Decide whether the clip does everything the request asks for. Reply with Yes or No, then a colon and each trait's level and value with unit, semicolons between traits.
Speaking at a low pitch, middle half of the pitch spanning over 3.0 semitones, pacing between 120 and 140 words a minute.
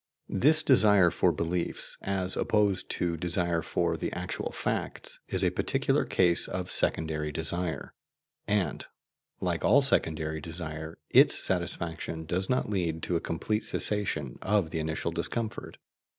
Yes: very low, 85 Hz; average, 3.4 semitones; slow, 135 wpm